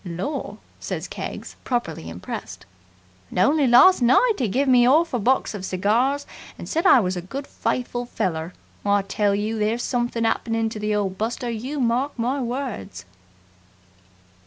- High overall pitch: Yes, high, 235 Hz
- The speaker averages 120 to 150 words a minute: No, average, 160 wpm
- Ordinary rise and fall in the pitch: Yes, average, 4.3 semitones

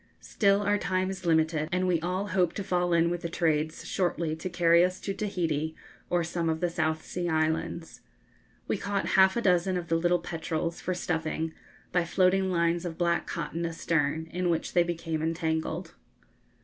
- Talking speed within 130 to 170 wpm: No, average, 185 wpm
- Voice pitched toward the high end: No, medium, 170 Hz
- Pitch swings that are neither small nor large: No, narrow, 2.0 semitones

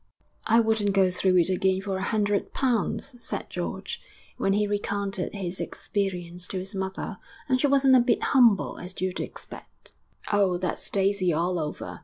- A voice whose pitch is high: Yes, high, 195 Hz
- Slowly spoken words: No, average, 175 wpm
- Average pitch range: No, narrow, 2.2 semitones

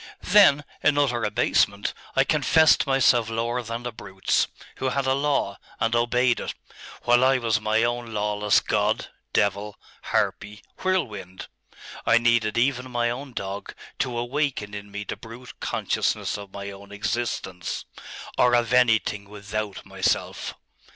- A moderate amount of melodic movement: Yes, average, 3.4 semitones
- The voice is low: Yes, low, 115 Hz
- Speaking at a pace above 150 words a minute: No, average, 145 wpm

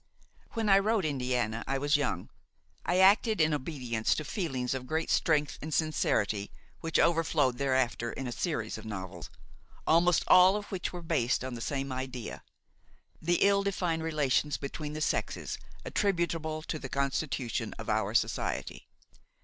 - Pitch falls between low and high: Yes, medium, 150 Hz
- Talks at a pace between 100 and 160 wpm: Yes, average, 155 wpm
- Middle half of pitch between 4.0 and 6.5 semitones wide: Yes, average, 4.8 semitones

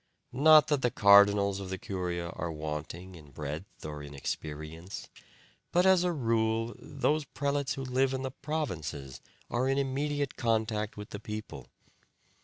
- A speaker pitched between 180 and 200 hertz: No, low, 110 Hz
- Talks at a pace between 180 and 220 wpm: No, average, 155 wpm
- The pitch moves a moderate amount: No, wide, 7.9 semitones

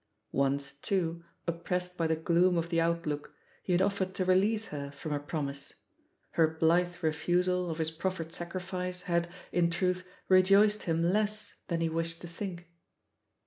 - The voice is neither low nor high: Yes, medium, 170 Hz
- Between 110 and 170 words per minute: Yes, average, 160 wpm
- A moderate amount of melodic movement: No, narrow, 2.1 semitones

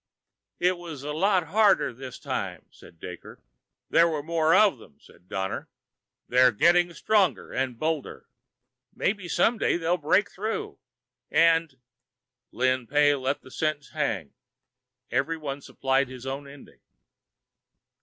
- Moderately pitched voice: Yes, medium, 150 Hz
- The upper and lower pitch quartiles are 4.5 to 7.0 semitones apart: Yes, average, 4.9 semitones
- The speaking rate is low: Yes, slow, 130 wpm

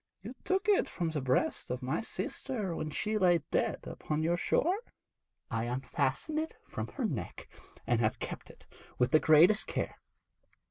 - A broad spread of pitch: Yes, wide, 9.0 semitones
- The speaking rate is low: No, average, 170 wpm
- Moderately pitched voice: Yes, medium, 165 Hz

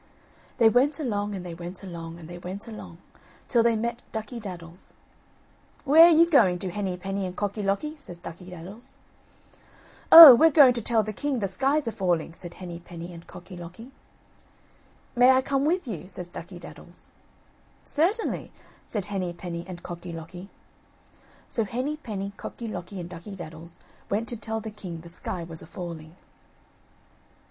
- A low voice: No, high, 195 Hz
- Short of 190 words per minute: Yes, average, 170 wpm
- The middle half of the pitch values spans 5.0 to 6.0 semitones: Yes, average, 5.3 semitones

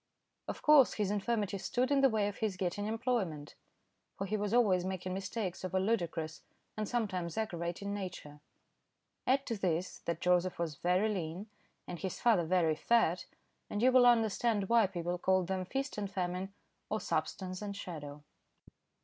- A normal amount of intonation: Yes, average, 3.7 semitones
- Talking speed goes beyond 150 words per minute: Yes, average, 165 wpm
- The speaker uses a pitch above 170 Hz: Yes, high, 190 Hz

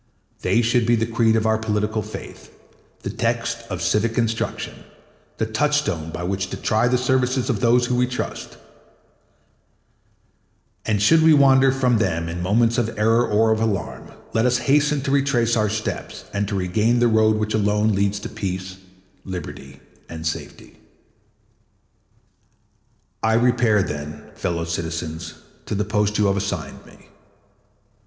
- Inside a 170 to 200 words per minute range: No, average, 155 wpm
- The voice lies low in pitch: Yes, low, 110 Hz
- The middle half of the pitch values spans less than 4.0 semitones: Yes, average, 3.5 semitones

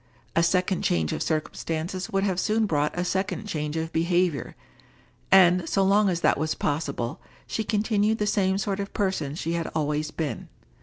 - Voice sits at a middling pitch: Yes, medium, 180 Hz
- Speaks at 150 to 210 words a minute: Yes, average, 175 wpm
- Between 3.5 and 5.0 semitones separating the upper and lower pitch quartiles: Yes, average, 4.0 semitones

